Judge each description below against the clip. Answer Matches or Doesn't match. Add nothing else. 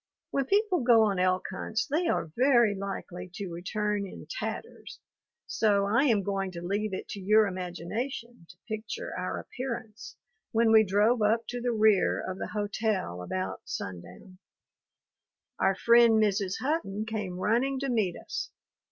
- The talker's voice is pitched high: Matches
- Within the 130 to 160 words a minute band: Matches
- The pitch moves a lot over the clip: Doesn't match